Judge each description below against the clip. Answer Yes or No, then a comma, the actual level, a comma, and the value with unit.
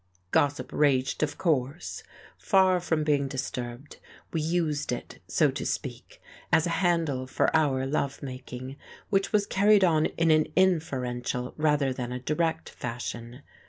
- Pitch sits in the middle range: Yes, medium, 145 Hz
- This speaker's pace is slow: No, average, 145 wpm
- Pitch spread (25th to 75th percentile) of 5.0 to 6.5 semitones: No, average, 4.3 semitones